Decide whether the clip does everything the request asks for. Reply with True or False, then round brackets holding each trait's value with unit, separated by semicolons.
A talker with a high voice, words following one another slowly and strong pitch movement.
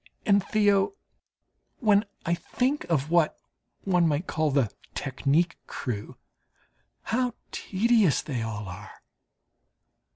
False (170 Hz; 105 wpm; 7.0 semitones)